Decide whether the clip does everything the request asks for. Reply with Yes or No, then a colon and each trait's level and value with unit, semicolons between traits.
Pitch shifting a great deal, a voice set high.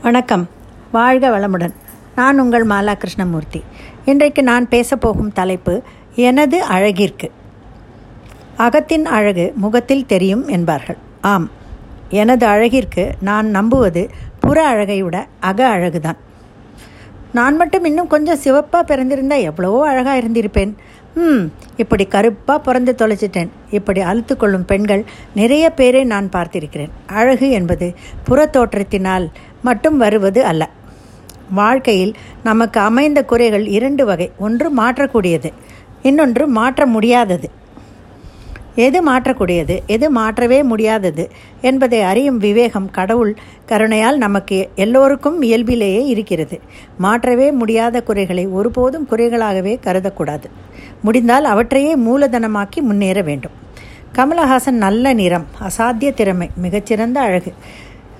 Yes: wide, 5.7 semitones; high, 220 Hz